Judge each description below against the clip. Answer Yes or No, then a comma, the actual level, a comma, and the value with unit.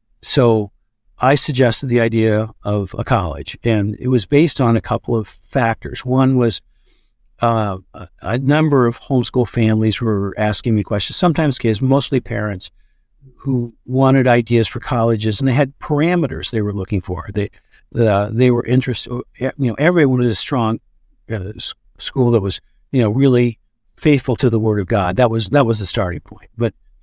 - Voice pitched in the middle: No, low, 115 Hz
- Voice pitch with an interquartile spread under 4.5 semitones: Yes, average, 3.2 semitones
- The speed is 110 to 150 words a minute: No, average, 175 wpm